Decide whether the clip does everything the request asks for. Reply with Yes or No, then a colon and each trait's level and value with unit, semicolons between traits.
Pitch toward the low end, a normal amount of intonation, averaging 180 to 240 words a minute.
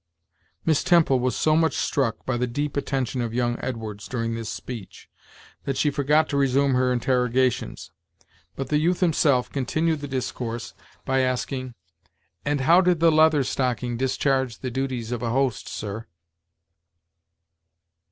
No: low, 130 Hz; average, 3.0 semitones; average, 150 wpm